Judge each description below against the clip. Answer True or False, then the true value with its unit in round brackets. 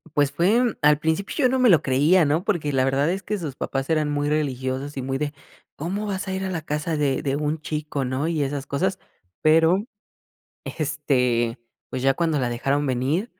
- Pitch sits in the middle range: True (150 Hz)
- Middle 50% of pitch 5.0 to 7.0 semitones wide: False (3.8 semitones)